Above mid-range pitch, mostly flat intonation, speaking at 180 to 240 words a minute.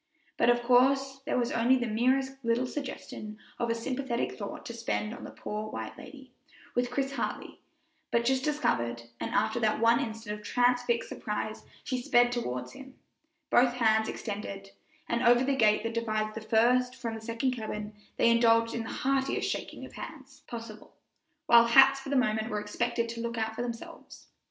Yes: high, 235 Hz; narrow, 2.3 semitones; average, 185 wpm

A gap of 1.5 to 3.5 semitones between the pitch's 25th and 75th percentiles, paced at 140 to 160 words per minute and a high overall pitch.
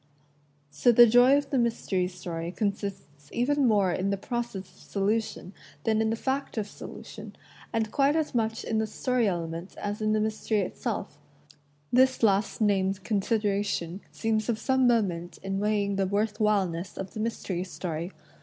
No: average, 3.1 semitones; average, 170 wpm; high, 210 Hz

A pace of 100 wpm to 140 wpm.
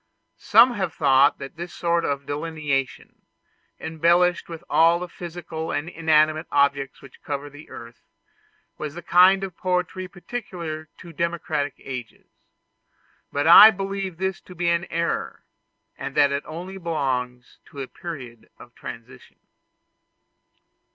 Yes: slow, 135 wpm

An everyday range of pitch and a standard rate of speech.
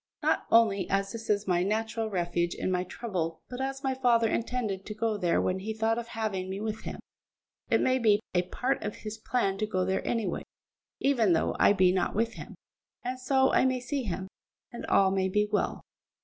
No: average, 3.8 semitones; fast, 215 wpm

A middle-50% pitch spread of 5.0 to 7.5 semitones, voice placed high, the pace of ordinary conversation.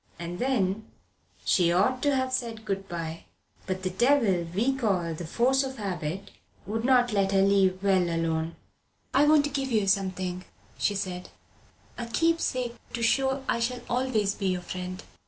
Yes: wide, 5.5 semitones; high, 200 Hz; average, 170 wpm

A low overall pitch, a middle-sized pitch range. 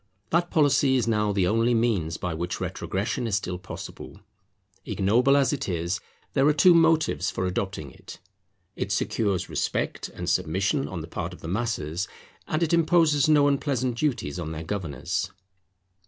No: low, 110 Hz; wide, 7.9 semitones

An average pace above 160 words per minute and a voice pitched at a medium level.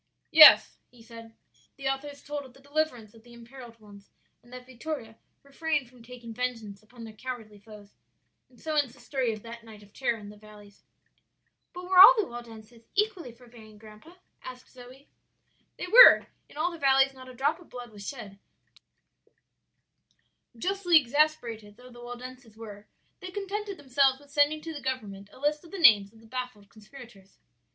No: average, 180 wpm; very high, 250 Hz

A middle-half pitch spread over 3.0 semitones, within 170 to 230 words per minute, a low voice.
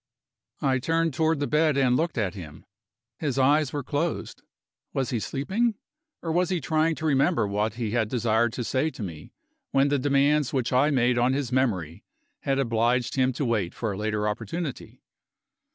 Yes: average, 4.5 semitones; average, 185 wpm; low, 130 Hz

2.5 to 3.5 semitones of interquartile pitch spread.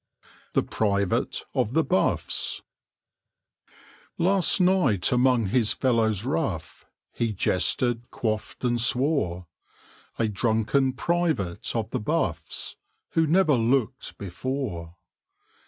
No: average, 4.7 semitones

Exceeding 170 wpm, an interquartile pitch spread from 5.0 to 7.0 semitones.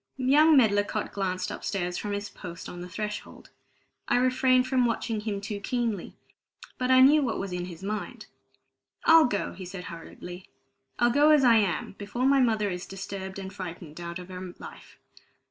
Yes: average, 180 wpm; average, 5.3 semitones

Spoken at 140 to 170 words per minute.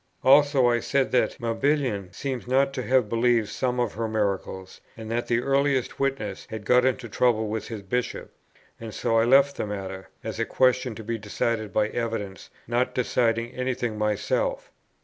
No: average, 180 wpm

